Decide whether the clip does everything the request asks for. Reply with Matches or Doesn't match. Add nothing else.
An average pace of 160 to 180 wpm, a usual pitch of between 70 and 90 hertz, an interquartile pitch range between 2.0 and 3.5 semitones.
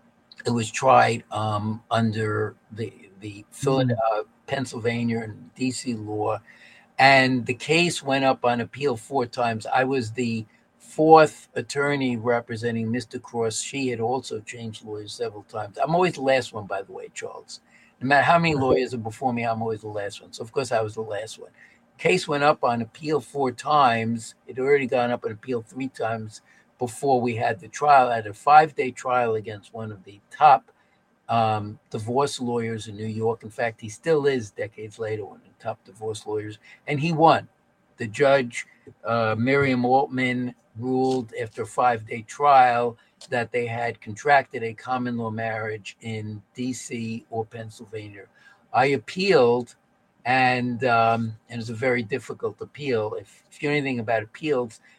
Doesn't match